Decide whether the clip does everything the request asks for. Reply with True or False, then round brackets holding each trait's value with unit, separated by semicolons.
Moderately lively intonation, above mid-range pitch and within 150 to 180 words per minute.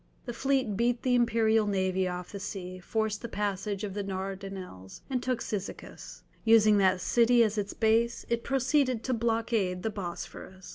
True (3.5 semitones; 215 Hz; 165 wpm)